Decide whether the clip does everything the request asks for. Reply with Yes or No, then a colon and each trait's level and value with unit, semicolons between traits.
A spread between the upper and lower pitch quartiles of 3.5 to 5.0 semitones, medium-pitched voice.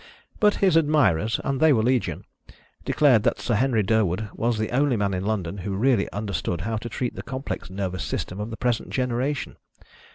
No: average, 4.5 semitones; low, 115 Hz